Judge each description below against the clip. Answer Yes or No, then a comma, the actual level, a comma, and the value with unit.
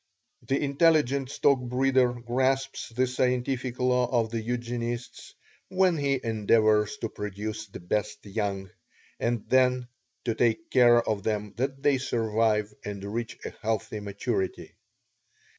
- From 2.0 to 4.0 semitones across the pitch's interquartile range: Yes, average, 3.2 semitones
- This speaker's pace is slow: Yes, slow, 125 wpm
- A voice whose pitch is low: Yes, low, 120 Hz